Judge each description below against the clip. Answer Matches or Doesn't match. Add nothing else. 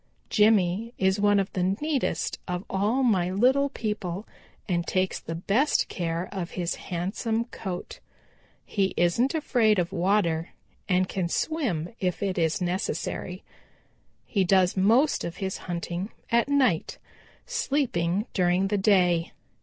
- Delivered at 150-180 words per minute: Doesn't match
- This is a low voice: Doesn't match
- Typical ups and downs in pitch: Matches